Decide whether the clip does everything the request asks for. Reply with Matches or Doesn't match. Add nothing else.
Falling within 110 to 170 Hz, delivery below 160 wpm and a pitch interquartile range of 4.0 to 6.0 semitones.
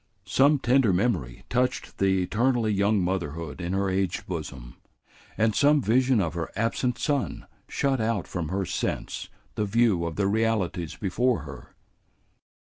Doesn't match